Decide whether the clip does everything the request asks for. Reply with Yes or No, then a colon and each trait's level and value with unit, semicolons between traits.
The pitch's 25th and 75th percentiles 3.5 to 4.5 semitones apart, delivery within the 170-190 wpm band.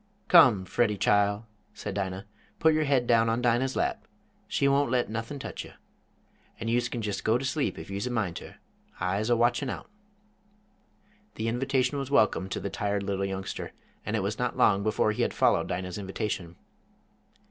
Yes: average, 3.9 semitones; average, 185 wpm